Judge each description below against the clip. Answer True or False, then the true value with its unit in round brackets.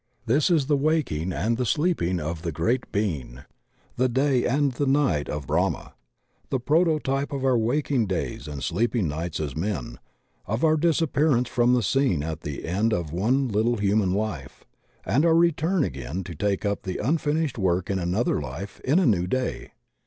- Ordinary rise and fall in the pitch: False (8.3 semitones)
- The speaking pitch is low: True (110 Hz)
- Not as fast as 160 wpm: False (180 wpm)